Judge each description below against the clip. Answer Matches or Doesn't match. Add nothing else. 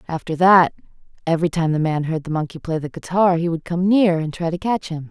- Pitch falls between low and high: Matches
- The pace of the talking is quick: Matches